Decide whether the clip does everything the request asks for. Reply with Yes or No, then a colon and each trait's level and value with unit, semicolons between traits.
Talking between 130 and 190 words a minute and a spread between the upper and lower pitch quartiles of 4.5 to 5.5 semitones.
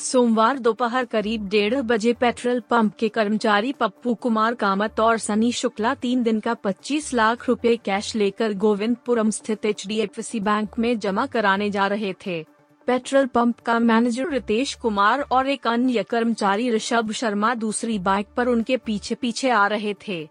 No: average, 160 wpm; narrow, 2.4 semitones